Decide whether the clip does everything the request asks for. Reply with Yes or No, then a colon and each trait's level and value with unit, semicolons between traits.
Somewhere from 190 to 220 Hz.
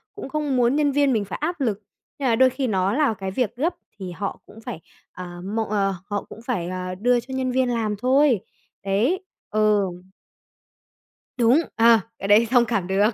No: high, 230 Hz